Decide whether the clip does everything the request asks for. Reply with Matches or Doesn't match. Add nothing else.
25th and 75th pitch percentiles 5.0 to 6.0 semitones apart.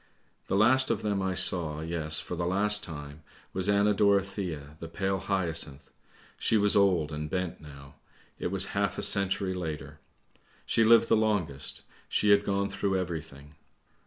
Doesn't match